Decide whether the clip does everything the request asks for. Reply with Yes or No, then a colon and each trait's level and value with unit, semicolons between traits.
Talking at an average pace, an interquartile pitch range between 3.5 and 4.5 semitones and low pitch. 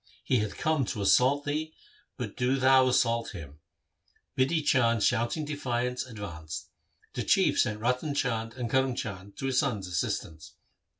Yes: average, 155 wpm; average, 3.9 semitones; low, 125 Hz